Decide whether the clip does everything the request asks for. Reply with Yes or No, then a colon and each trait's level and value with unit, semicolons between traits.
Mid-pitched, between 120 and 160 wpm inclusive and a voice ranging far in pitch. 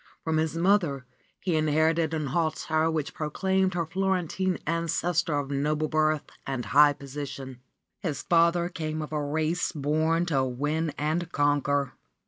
No: medium, 155 Hz; average, 140 wpm; narrow, 2.5 semitones